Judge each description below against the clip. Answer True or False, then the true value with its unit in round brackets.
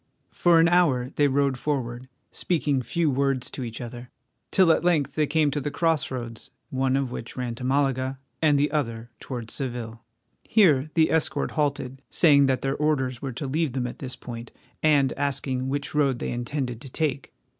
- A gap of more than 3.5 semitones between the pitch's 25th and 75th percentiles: False (2.9 semitones)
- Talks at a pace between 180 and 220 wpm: True (190 wpm)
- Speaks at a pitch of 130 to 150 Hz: True (135 Hz)